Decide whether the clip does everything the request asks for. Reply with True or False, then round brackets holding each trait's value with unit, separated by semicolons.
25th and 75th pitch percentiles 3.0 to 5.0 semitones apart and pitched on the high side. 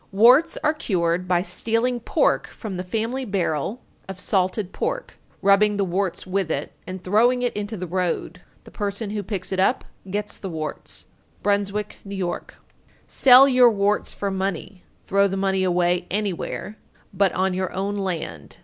False (2.5 semitones; 195 Hz)